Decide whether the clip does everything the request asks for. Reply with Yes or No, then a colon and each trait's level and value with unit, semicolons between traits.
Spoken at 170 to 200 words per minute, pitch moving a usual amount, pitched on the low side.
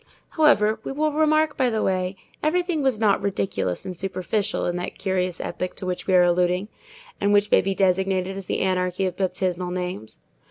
No: average, 190 wpm; average, 3.0 semitones; high, 190 Hz